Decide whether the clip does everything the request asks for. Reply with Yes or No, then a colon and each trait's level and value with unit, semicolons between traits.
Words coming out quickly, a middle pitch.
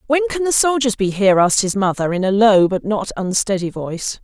No: fast, 225 wpm; high, 210 Hz